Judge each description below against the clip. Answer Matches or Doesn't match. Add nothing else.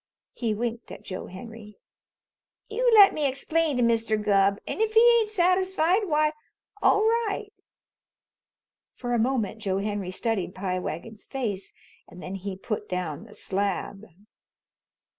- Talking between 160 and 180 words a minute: Doesn't match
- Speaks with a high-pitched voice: Matches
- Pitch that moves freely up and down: Matches